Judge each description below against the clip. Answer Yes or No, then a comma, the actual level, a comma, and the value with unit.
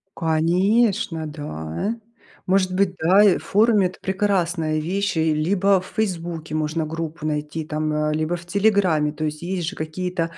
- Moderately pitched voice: Yes, medium, 170 Hz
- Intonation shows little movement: No, average, 3.6 semitones